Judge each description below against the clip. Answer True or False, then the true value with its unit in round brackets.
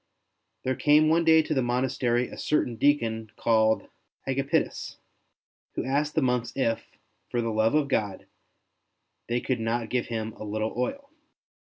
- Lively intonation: False (3.7 semitones)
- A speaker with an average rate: True (155 wpm)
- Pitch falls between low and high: False (120 Hz)